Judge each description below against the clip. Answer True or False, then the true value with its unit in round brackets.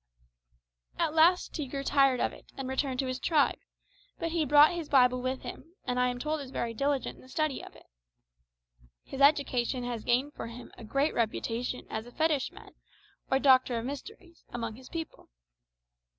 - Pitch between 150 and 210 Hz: False (265 Hz)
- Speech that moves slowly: False (185 wpm)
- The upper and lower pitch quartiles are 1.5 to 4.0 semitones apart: True (3.3 semitones)